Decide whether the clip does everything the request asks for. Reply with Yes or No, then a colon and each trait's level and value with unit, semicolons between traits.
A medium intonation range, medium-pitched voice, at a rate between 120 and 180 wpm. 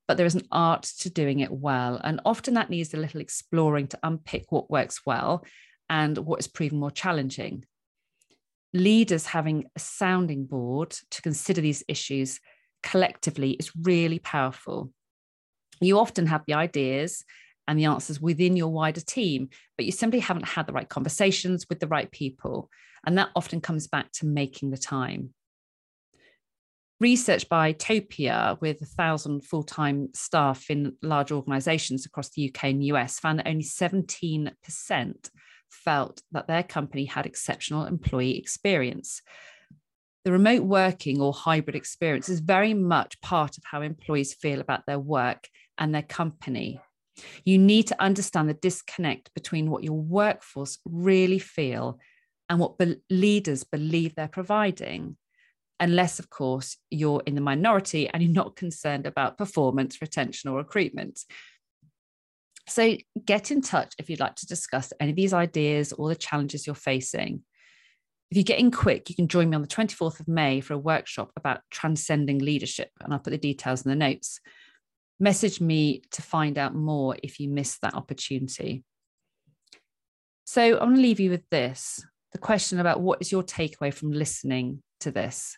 Yes: average, 4.2 semitones; medium, 155 Hz; average, 165 wpm